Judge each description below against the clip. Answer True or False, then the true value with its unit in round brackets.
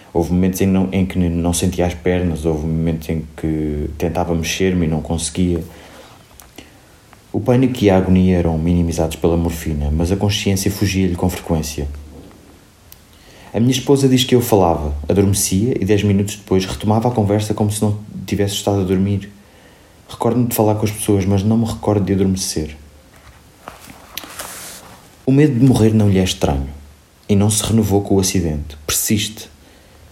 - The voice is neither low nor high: False (95 Hz)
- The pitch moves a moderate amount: True (3.8 semitones)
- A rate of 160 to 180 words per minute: True (165 wpm)